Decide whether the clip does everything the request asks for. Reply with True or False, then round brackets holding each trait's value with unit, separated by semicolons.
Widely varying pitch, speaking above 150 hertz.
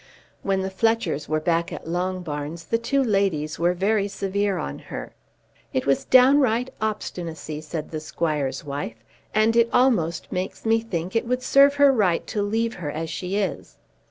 True (6.1 semitones; 190 Hz)